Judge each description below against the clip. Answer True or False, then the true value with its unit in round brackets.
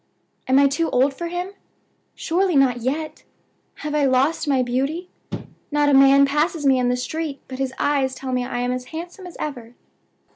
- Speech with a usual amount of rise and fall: True (3.6 semitones)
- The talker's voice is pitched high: True (275 Hz)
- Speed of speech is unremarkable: True (190 wpm)